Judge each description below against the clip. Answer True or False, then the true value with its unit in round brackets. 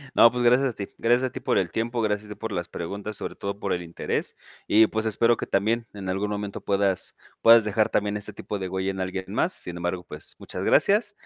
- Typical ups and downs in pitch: True (3.1 semitones)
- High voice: False (105 Hz)